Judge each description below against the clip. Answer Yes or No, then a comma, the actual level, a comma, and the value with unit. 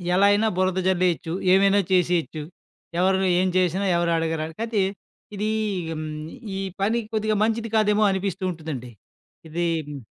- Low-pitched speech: No, medium, 185 Hz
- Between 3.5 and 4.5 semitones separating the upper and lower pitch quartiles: Yes, average, 3.9 semitones